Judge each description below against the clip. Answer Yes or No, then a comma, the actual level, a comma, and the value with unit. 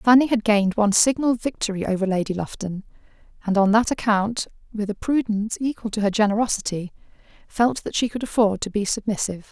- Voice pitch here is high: Yes, high, 215 Hz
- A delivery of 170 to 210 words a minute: Yes, average, 175 wpm